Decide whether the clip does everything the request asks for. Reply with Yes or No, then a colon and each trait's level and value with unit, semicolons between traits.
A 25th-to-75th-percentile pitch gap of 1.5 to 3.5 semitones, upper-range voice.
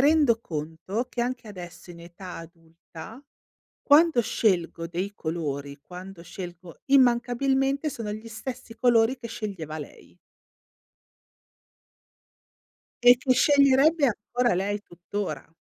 No: wide, 6.5 semitones; high, 215 Hz